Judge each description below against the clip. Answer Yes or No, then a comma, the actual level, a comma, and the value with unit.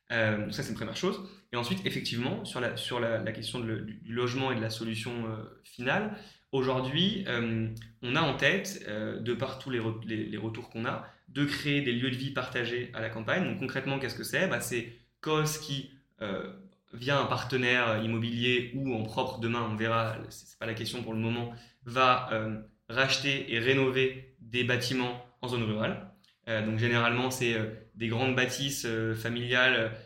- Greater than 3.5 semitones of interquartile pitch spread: No, average, 2.7 semitones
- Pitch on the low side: Yes, low, 120 Hz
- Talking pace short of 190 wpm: No, average, 195 wpm